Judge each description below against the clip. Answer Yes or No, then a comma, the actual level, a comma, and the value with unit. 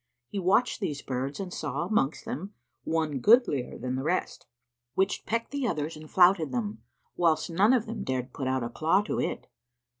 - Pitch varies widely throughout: Yes, wide, 6.7 semitones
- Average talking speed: Yes, average, 185 wpm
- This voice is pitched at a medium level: Yes, medium, 160 Hz